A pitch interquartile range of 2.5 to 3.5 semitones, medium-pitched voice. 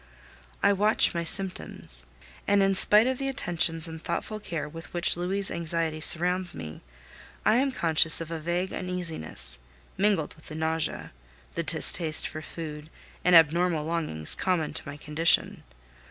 Yes: average, 2.9 semitones; medium, 170 Hz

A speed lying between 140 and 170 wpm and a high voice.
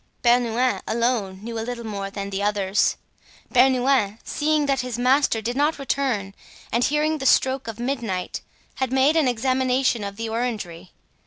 Yes: average, 160 wpm; high, 240 Hz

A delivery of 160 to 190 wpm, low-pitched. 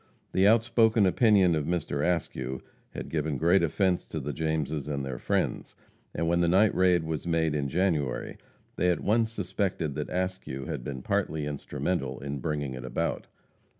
Yes: average, 170 wpm; very low, 80 Hz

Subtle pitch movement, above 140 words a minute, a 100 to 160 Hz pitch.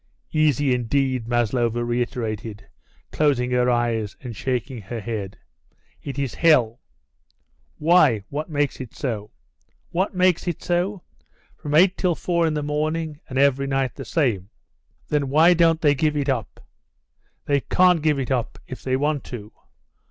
No: average, 4.5 semitones; average, 150 wpm; low, 135 Hz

